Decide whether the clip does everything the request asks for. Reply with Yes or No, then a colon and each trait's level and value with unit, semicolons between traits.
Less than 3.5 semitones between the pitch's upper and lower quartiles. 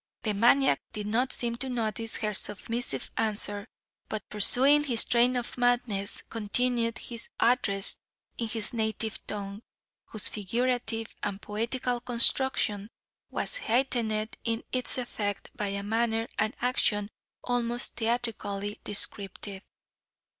Yes: average, 2.8 semitones